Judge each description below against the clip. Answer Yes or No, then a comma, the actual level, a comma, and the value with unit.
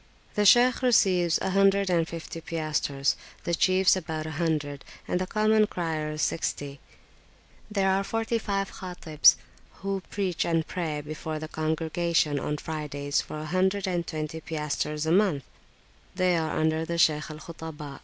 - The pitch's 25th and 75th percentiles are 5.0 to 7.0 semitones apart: No, average, 3.5 semitones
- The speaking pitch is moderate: Yes, medium, 165 Hz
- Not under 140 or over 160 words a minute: Yes, average, 155 wpm